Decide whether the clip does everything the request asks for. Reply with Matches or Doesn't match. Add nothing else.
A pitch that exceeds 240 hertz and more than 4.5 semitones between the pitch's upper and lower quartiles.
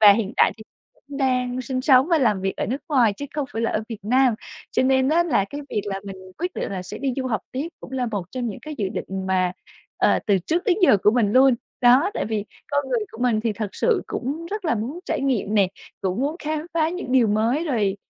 Matches